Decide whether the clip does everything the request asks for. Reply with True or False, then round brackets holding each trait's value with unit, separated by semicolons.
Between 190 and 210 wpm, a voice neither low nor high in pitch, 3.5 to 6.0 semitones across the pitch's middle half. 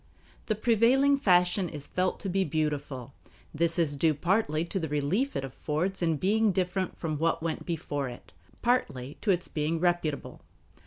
False (165 wpm; 170 Hz; 4.4 semitones)